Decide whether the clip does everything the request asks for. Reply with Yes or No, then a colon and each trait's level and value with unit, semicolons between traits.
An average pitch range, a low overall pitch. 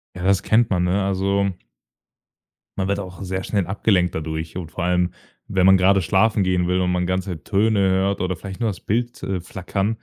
No: narrow, 1.7 semitones; very low, 95 Hz